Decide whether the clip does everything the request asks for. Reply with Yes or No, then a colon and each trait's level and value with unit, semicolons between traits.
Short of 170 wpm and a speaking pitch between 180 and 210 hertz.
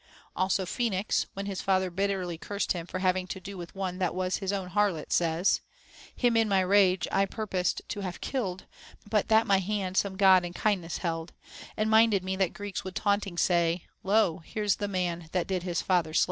No: average, 200 wpm; high, 190 Hz